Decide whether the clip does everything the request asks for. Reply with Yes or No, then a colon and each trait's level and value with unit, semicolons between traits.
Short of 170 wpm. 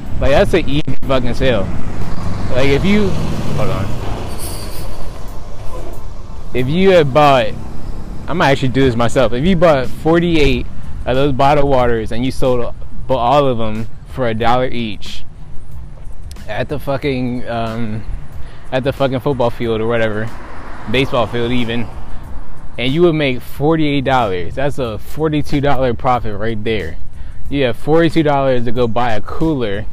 Yes: average, 145 wpm